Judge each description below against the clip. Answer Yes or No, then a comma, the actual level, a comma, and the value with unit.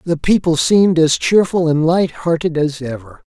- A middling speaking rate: Yes, average, 165 wpm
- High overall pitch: No, medium, 160 Hz